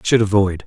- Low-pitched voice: Yes, low, 100 Hz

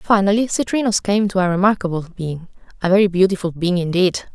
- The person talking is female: Yes, female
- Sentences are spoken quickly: No, average, 165 wpm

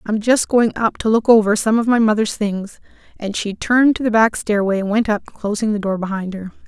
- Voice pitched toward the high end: Yes, high, 215 Hz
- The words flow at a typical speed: No, fast, 245 wpm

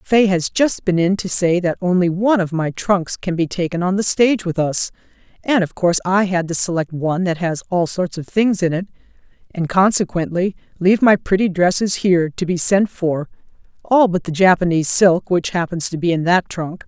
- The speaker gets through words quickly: Yes, fast, 210 wpm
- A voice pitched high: No, medium, 180 Hz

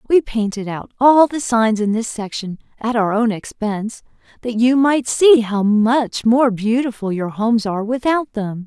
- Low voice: No, high, 230 Hz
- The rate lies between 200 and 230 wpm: No, average, 180 wpm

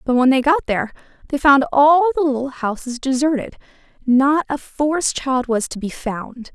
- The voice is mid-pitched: No, very high, 270 Hz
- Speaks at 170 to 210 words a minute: Yes, average, 185 wpm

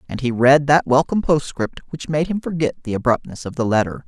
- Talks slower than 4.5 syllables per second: No, 5.9 syllables/s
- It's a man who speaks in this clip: Yes, male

